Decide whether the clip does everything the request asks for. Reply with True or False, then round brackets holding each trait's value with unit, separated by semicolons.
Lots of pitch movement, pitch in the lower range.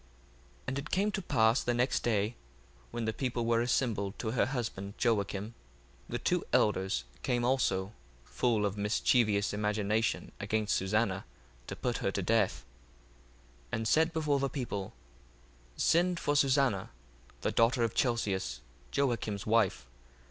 False (3.9 semitones; 115 Hz)